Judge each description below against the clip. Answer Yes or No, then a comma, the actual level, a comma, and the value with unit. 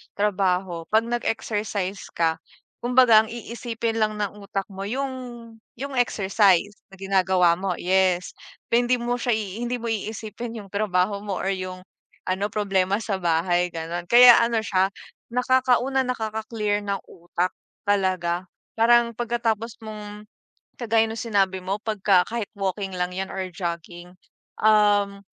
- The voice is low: No, high, 205 Hz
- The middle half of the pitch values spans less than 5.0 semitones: Yes, average, 3.3 semitones